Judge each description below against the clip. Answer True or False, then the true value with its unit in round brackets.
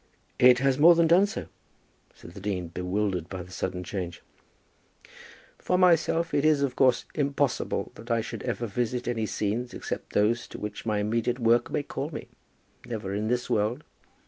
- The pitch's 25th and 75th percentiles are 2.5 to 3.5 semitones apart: False (5.0 semitones)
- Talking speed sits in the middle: True (175 wpm)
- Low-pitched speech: True (115 Hz)